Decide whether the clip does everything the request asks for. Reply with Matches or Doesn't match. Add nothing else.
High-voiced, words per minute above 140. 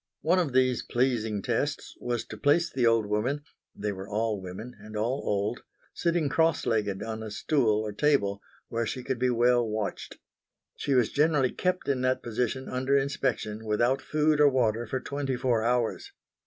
Doesn't match